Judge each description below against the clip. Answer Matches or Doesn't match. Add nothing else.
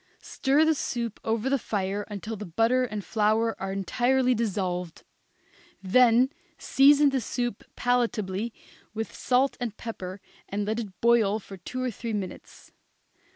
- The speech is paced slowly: Doesn't match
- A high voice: Matches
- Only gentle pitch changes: Doesn't match